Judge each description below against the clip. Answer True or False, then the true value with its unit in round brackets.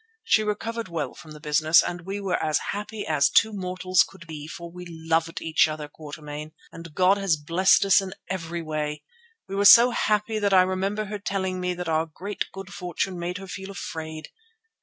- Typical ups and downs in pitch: True (3.7 semitones)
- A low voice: False (180 Hz)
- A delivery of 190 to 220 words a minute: True (200 wpm)